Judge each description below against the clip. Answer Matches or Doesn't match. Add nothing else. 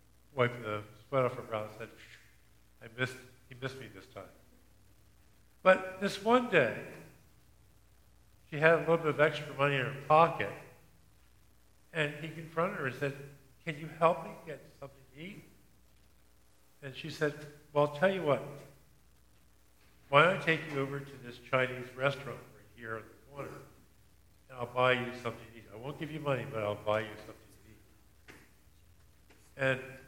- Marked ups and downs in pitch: Matches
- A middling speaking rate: Matches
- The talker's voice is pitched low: Matches